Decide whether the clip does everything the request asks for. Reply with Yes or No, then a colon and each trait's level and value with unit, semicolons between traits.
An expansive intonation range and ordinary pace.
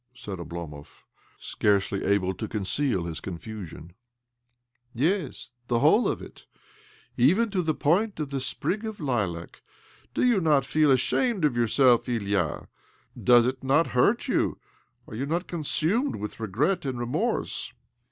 Yes: wide, 7.6 semitones; average, 155 wpm